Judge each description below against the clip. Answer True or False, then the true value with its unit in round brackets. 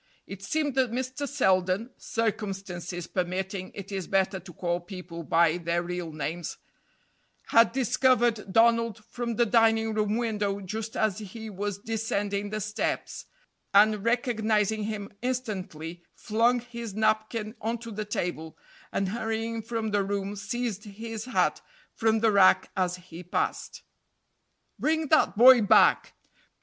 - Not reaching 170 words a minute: True (135 wpm)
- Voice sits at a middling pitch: False (215 Hz)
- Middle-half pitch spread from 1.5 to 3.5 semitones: True (3.2 semitones)